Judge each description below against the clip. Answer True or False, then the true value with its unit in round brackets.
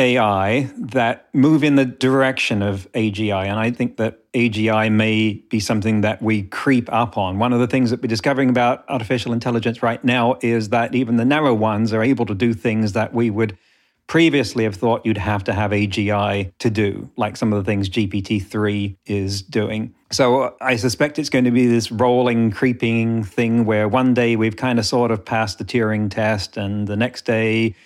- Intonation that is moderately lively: False (2.3 semitones)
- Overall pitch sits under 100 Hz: False (115 Hz)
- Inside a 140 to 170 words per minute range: False (200 wpm)